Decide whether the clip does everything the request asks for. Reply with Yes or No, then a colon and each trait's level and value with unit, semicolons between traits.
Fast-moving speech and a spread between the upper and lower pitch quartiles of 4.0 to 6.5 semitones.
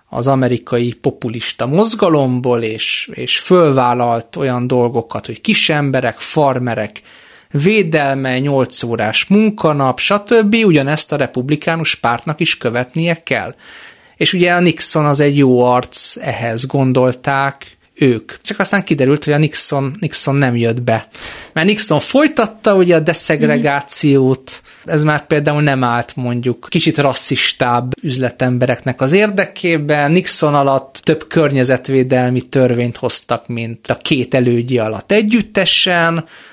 No: average, 125 wpm; average, 4.8 semitones